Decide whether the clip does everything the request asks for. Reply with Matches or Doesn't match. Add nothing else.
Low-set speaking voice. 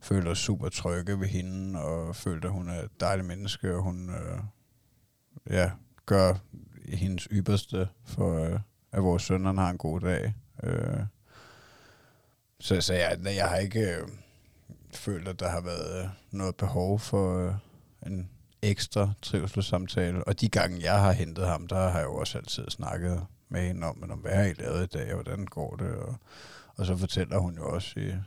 Matches